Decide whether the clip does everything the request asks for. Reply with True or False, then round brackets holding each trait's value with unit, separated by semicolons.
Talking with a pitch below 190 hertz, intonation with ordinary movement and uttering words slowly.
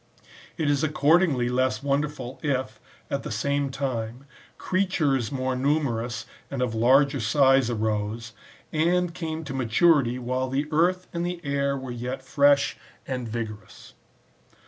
True (135 Hz; 3.5 semitones; 130 wpm)